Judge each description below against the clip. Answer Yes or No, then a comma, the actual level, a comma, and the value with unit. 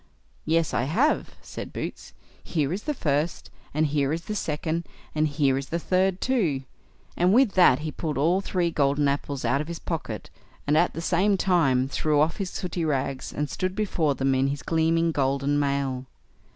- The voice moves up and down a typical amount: Yes, average, 3.9 semitones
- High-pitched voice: No, medium, 155 Hz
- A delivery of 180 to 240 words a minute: Yes, average, 190 wpm